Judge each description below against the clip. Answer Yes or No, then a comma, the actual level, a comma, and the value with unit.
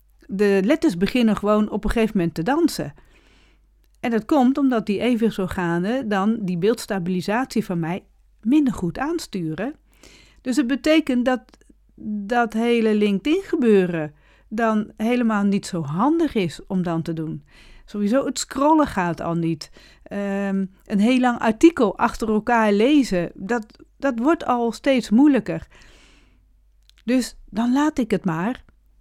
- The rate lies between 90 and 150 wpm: Yes, average, 140 wpm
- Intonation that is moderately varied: Yes, average, 5.0 semitones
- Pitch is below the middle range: No, high, 220 Hz